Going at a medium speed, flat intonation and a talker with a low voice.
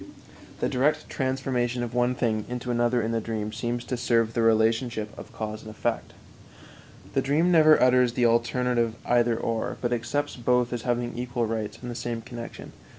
Yes: average, 180 wpm; narrow, 1.5 semitones; low, 120 Hz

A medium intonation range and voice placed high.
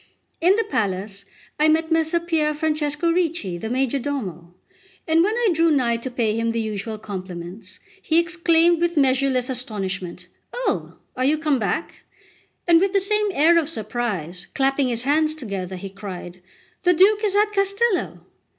No: wide, 7.9 semitones; very high, 280 Hz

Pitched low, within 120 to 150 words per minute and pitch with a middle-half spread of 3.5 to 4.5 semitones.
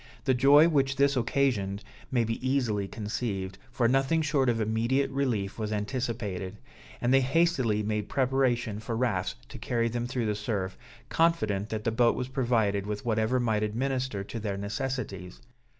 No: low, 115 Hz; average, 165 wpm; average, 4.0 semitones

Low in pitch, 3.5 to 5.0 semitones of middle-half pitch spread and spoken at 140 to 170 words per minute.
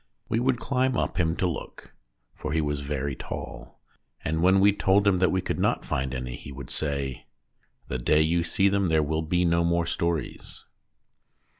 No: very low, 85 Hz; average, 4.4 semitones; average, 190 wpm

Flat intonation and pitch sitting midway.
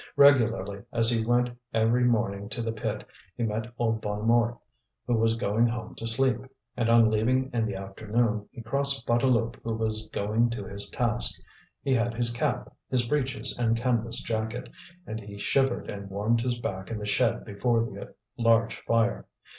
No: narrow, 1.8 semitones; low, 115 Hz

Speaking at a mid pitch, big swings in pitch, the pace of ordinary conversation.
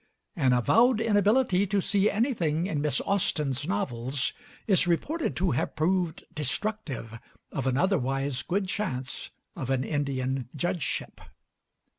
No: medium, 165 Hz; wide, 7.0 semitones; slow, 125 wpm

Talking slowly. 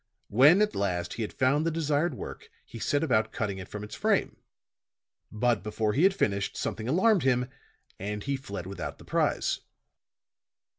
No: average, 170 wpm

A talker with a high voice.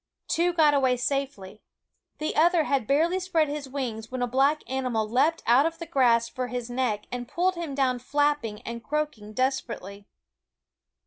Yes: very high, 265 Hz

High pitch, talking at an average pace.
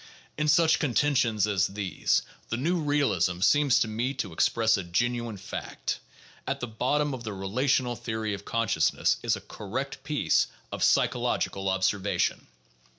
No: low, 115 Hz; average, 150 wpm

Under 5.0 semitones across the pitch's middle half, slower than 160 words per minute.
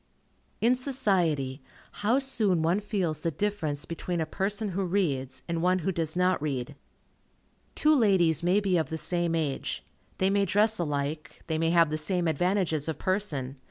No: average, 4.2 semitones; average, 170 wpm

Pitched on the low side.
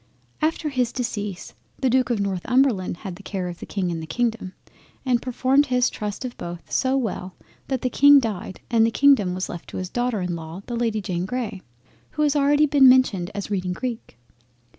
No: high, 225 Hz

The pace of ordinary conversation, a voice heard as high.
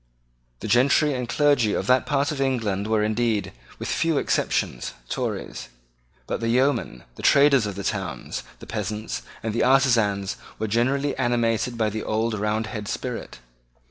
No: average, 155 wpm; low, 115 Hz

